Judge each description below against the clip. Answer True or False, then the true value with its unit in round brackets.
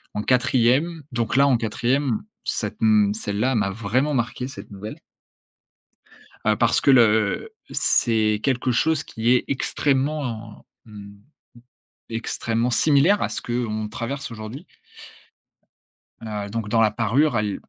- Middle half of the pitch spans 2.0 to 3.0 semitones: False (3.6 semitones)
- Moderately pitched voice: False (115 Hz)